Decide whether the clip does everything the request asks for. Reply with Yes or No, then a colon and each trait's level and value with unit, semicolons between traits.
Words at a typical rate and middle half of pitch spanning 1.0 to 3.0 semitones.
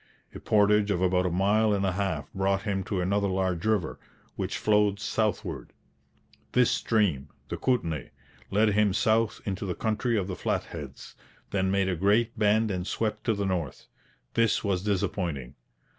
Yes: average, 165 wpm; narrow, 2.4 semitones